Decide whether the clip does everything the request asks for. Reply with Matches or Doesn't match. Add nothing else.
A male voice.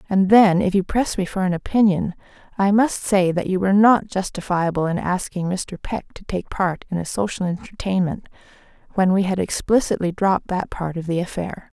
Doesn't match